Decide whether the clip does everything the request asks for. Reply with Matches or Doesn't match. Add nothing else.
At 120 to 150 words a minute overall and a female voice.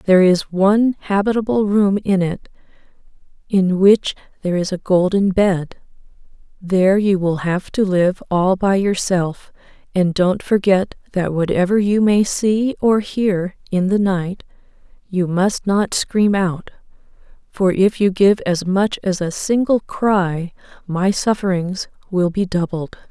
Matches